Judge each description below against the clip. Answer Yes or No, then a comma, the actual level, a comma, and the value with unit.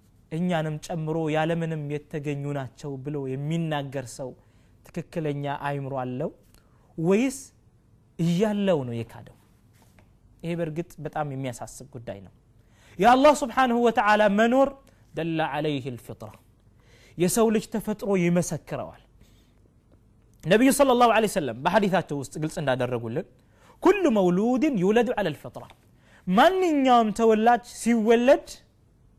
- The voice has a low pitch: No, medium, 155 Hz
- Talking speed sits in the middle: Yes, average, 100 wpm